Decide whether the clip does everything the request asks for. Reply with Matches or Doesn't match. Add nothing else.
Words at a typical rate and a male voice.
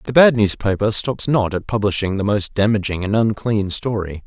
Matches